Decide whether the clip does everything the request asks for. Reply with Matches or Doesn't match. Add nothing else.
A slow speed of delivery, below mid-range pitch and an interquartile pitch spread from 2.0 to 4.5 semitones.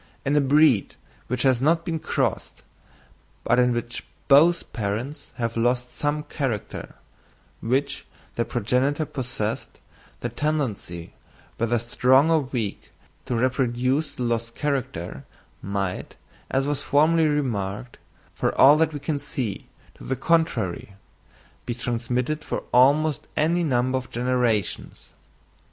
Matches